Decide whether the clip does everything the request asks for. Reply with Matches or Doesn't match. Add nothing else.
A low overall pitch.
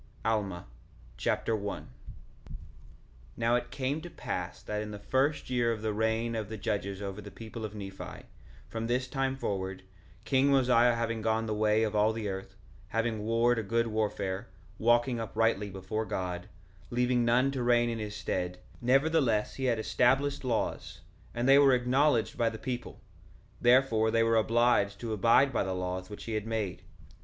Matches